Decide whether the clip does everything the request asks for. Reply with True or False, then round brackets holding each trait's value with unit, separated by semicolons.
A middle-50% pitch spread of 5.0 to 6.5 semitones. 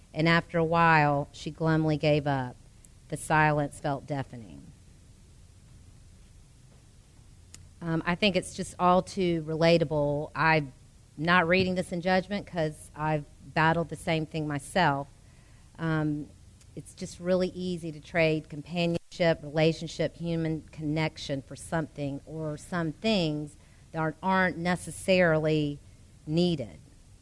False (3.3 semitones)